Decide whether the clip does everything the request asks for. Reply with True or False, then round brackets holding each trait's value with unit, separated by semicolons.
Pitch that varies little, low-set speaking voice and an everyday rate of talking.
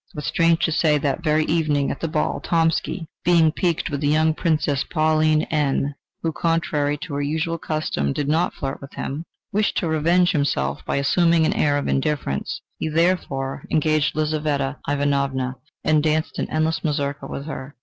False (2.2 semitones; 155 Hz; 175 wpm)